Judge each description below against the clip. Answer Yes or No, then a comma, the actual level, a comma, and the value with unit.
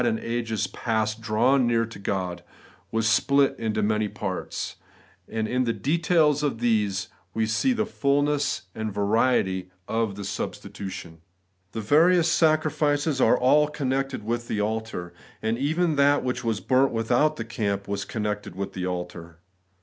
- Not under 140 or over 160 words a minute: Yes, average, 155 wpm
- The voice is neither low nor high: No, low, 115 Hz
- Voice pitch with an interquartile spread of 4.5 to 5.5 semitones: Yes, average, 5.1 semitones